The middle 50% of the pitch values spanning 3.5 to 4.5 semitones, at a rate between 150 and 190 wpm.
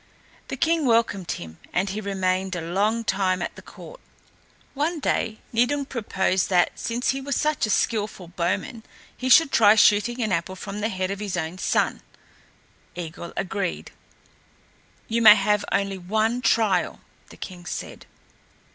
Yes: average, 3.8 semitones; average, 155 wpm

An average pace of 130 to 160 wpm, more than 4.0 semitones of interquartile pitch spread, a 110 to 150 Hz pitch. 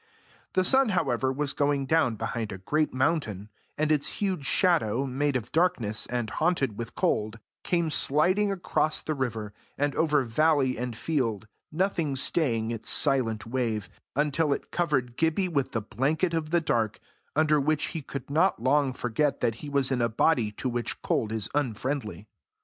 No: average, 170 wpm; average, 5.0 semitones; medium, 140 Hz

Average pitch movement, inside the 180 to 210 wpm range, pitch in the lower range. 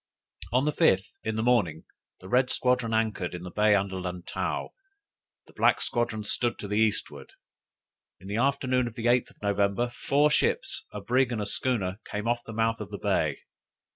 Yes: average, 3.6 semitones; average, 190 wpm; low, 110 Hz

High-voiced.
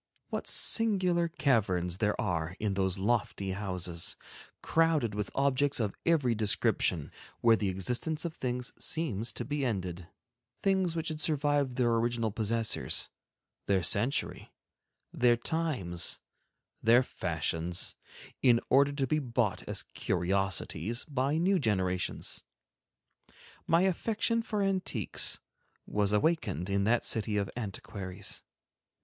No: low, 115 Hz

